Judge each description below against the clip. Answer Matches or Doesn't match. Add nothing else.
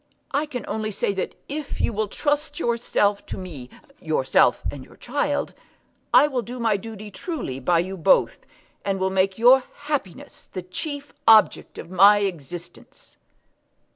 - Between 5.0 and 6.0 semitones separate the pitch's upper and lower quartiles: Matches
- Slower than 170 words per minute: Matches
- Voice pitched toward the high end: Matches